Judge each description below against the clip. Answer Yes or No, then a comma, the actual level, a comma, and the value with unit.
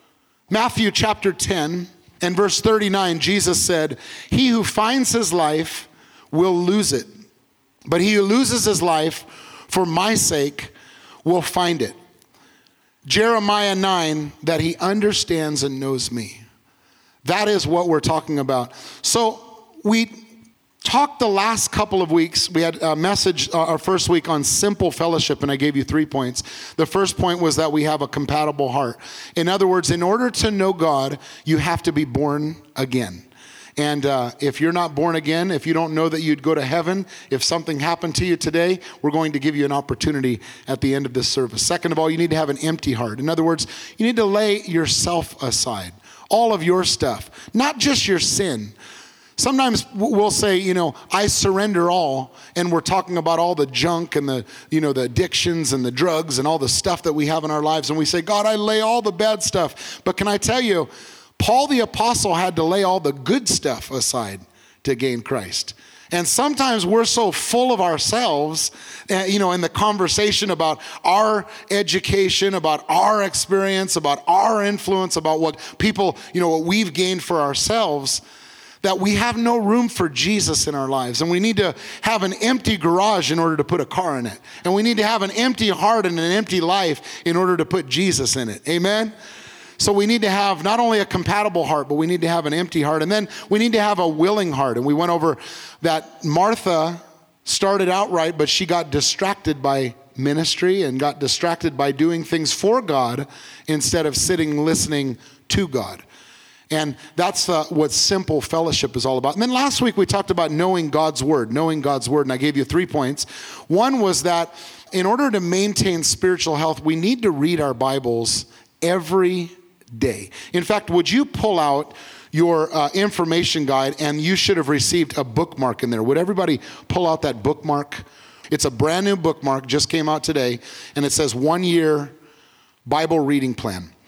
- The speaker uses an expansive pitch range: No, average, 4.7 semitones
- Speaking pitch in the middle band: Yes, medium, 165 Hz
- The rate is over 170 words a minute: Yes, average, 195 wpm